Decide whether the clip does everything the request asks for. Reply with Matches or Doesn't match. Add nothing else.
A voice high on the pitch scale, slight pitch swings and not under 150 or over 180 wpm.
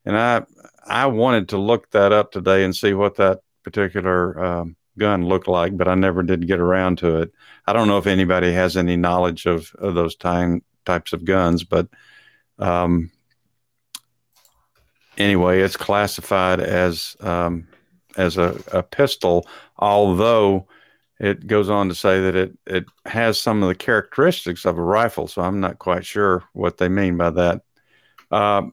Doesn't match